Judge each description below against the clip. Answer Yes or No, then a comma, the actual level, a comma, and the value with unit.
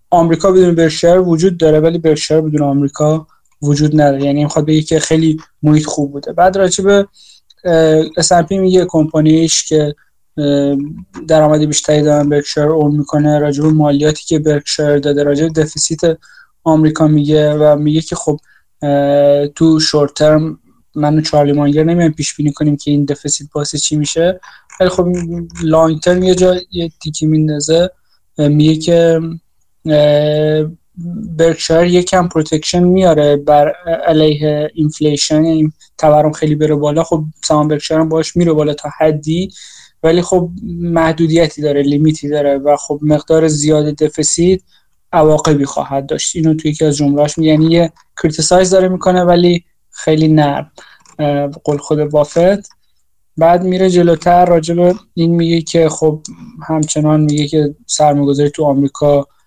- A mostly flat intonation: Yes, narrow, 2.0 semitones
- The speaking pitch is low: No, medium, 155 Hz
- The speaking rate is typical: Yes, average, 140 wpm